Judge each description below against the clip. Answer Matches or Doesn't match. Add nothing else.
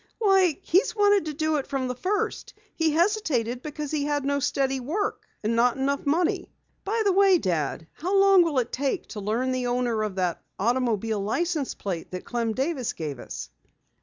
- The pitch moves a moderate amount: Doesn't match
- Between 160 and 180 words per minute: Doesn't match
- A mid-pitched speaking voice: Doesn't match